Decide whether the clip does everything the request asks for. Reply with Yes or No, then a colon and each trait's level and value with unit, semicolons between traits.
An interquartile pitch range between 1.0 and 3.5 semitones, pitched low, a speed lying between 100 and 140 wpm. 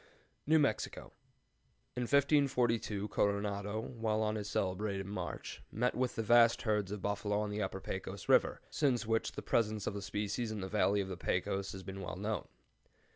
No: narrow, 2.5 semitones; low, 105 Hz; average, 175 wpm